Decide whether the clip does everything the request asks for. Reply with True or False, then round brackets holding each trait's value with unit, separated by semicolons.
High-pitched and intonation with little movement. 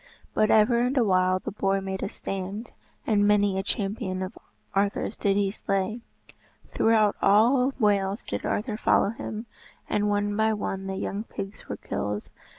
True (205 Hz; 2.0 semitones)